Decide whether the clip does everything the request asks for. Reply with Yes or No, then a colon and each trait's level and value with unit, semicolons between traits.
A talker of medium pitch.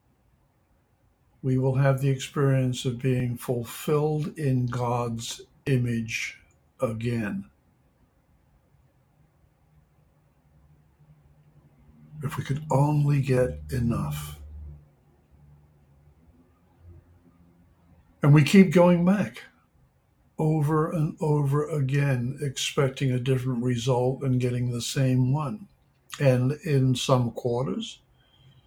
No: low, 125 Hz